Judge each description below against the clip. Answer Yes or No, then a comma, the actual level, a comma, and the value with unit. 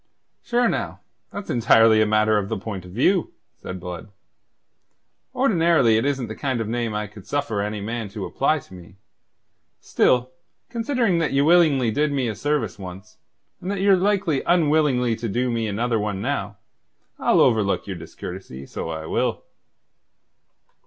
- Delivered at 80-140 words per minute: No, average, 160 wpm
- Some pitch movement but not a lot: No, wide, 6.5 semitones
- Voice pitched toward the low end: Yes, low, 115 Hz